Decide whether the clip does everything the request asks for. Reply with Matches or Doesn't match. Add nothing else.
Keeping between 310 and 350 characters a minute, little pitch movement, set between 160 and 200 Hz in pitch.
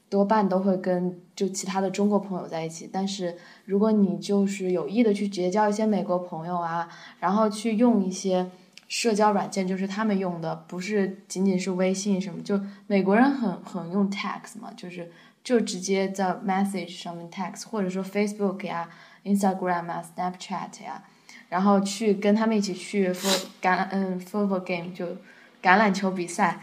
Matches